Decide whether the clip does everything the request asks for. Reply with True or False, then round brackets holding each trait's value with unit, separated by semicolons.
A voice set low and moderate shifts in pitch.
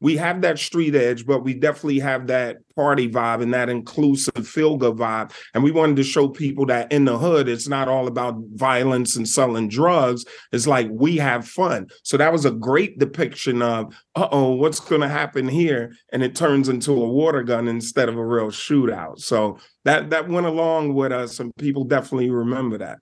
True (130 Hz; 3.4 semitones)